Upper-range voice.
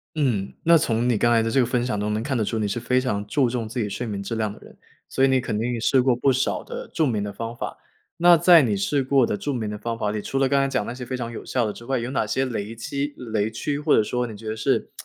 No: low, 120 Hz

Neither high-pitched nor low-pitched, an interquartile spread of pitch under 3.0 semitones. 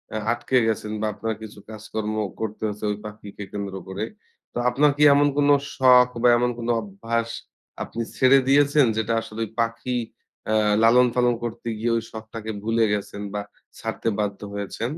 No: low, 115 Hz; narrow, 2.6 semitones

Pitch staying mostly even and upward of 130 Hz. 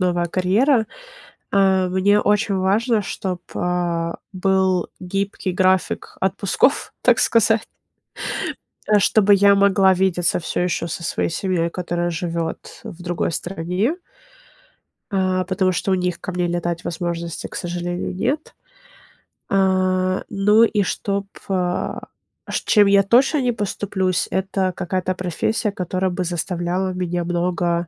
Yes: narrow, 2.0 semitones; medium, 185 Hz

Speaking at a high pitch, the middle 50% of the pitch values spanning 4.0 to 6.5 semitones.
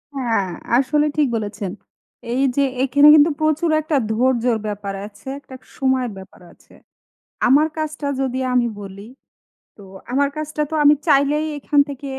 Yes: very high, 270 Hz; average, 4.3 semitones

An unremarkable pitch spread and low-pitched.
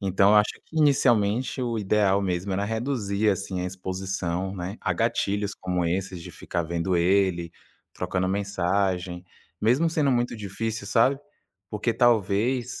Yes: average, 3.5 semitones; low, 100 Hz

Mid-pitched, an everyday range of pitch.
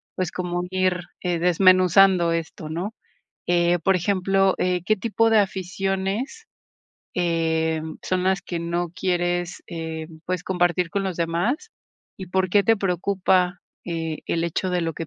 No: medium, 180 Hz; narrow, 2.0 semitones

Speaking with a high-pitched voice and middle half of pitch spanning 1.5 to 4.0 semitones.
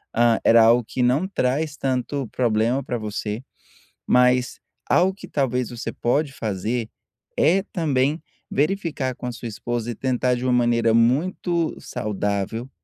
No: low, 125 Hz; average, 3.3 semitones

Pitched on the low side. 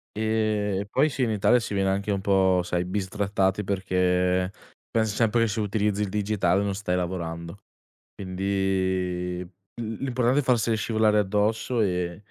Yes: low, 100 Hz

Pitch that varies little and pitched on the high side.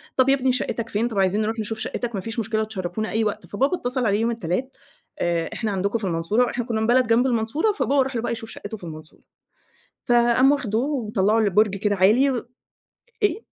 No: average, 3.2 semitones; high, 225 Hz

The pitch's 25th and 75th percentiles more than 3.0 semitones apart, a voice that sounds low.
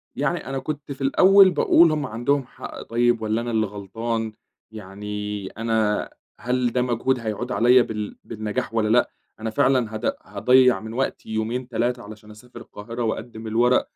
No: narrow, 2.6 semitones; low, 115 Hz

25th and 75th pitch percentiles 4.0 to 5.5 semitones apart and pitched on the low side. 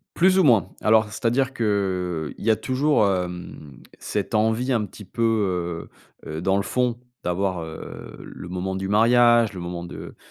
Yes: average, 4.6 semitones; low, 100 Hz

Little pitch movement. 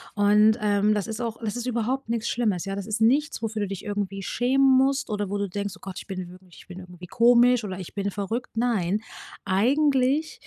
No: average, 3.6 semitones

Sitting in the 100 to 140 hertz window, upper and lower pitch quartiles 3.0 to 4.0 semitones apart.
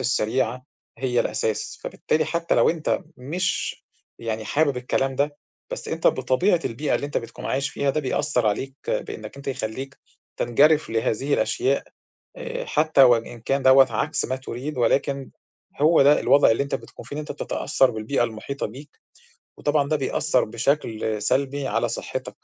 Yes: low, 135 Hz; average, 3.4 semitones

